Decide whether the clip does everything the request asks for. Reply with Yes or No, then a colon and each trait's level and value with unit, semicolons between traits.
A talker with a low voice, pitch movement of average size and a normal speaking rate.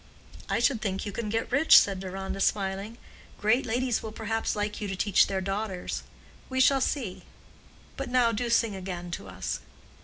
No: high, 210 Hz; average, 3.3 semitones; average, 180 wpm